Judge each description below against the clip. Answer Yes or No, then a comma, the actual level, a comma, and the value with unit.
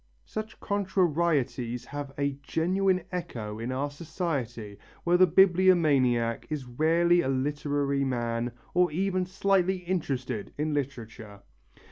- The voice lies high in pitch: No, medium, 145 Hz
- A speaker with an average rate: No, slow, 115 wpm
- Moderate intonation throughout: No, wide, 6.1 semitones